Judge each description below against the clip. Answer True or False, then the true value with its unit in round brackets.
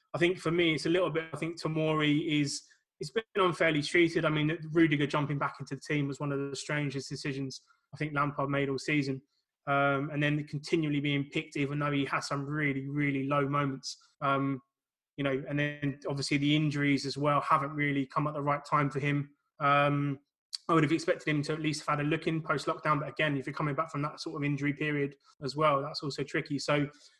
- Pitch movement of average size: False (1.7 semitones)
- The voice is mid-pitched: True (145 Hz)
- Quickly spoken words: True (230 wpm)